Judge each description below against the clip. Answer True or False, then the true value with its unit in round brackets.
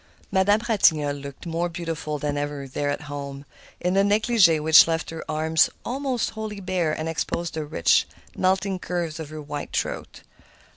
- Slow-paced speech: False (165 wpm)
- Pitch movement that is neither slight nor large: True (4.1 semitones)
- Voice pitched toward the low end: False (165 Hz)